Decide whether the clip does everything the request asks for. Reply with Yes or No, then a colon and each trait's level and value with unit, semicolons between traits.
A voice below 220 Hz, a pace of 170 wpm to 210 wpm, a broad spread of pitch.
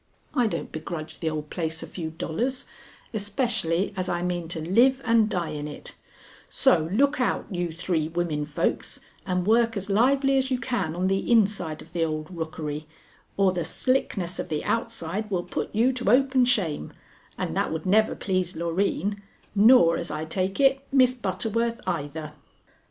Yes: medium, 185 Hz; average, 175 wpm; wide, 6.1 semitones